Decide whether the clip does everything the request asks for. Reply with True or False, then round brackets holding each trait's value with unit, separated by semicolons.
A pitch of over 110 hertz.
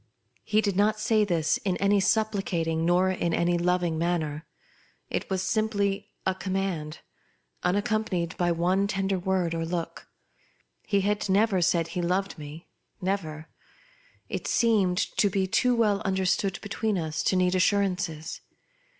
True (190 Hz)